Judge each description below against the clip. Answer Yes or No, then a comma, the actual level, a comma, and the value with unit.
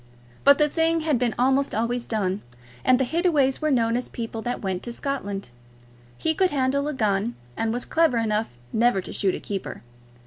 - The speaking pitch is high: Yes, high, 245 Hz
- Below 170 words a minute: No, average, 195 wpm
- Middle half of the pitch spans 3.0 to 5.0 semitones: Yes, average, 4.3 semitones